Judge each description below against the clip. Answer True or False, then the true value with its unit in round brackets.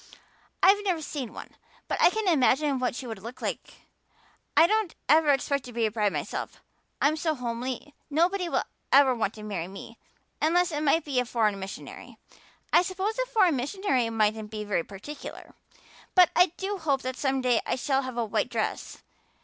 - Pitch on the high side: True (270 Hz)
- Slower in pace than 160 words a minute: False (190 wpm)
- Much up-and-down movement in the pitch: True (6.3 semitones)